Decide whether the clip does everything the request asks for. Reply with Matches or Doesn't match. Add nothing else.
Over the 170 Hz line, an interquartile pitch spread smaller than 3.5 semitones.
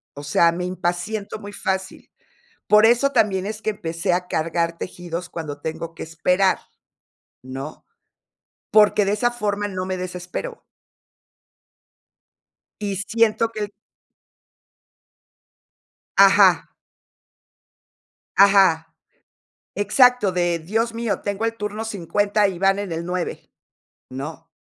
Doesn't match